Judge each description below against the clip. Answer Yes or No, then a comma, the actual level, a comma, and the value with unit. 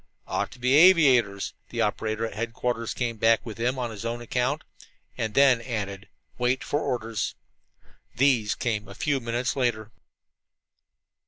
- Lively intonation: No, narrow, 2.4 semitones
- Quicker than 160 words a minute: No, average, 150 wpm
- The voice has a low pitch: Yes, low, 120 Hz